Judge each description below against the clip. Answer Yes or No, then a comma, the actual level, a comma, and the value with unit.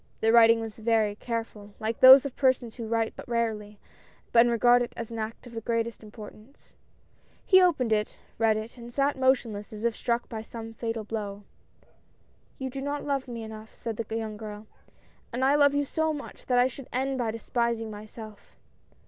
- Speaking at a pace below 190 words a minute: No, average, 200 wpm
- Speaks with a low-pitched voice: No, high, 230 Hz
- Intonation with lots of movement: No, narrow, 2.4 semitones